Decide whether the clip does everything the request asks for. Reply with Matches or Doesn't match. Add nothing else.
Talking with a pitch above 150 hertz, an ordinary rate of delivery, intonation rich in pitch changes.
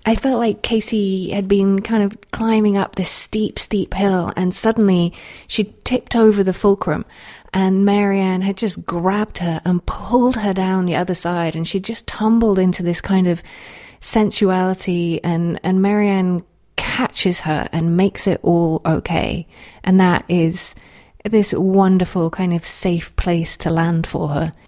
Doesn't match